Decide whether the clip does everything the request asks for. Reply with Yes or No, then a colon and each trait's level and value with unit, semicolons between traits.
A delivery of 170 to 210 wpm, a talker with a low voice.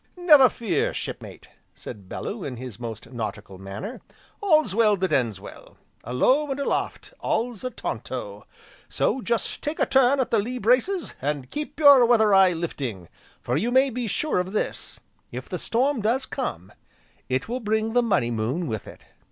No: average, 175 wpm; high, 215 Hz